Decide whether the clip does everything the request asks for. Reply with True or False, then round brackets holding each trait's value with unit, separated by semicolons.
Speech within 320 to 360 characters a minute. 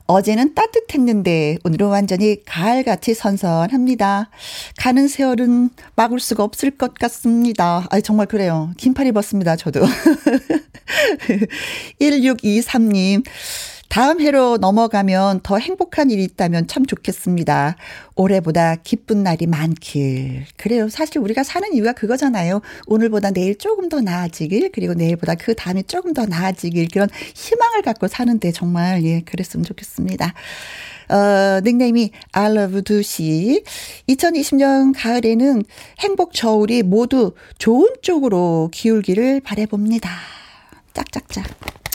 False (285 characters per minute)